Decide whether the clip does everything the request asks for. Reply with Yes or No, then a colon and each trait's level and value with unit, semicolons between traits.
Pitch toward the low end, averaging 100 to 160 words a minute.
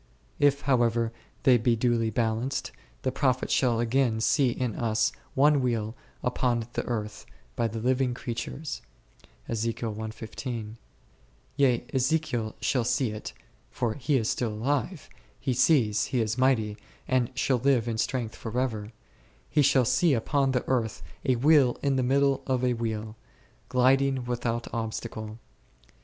Yes: low, 120 Hz; average, 145 wpm